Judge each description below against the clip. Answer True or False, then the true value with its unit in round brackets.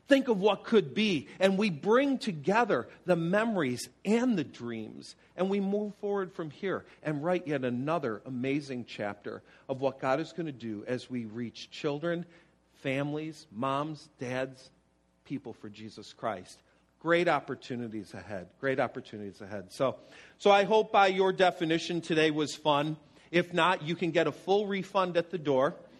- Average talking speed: True (165 wpm)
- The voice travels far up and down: True (6.5 semitones)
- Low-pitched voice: False (155 Hz)